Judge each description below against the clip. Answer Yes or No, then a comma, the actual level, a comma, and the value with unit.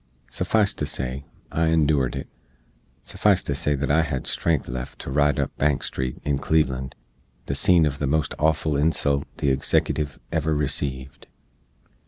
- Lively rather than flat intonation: No, average, 2.7 semitones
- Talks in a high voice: No, very low, 70 Hz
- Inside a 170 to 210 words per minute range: No, average, 160 wpm